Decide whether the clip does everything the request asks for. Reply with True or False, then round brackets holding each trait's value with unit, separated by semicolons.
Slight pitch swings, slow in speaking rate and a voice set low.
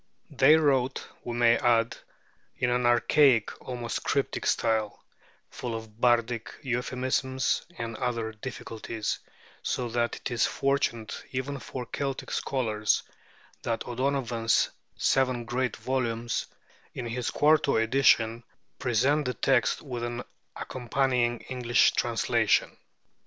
True (2.1 semitones; 115 wpm; 120 Hz)